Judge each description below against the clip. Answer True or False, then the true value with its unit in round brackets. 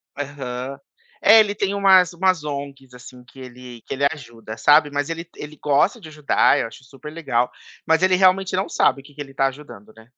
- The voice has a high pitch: False (145 Hz)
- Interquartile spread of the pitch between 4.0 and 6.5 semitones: True (4.6 semitones)